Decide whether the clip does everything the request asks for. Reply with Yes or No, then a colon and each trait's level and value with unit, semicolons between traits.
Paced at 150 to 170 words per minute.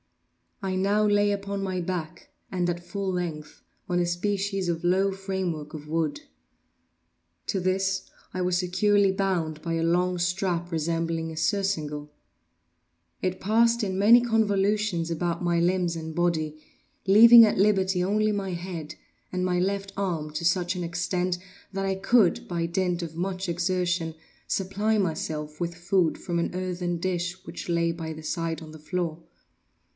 Yes: average, 155 wpm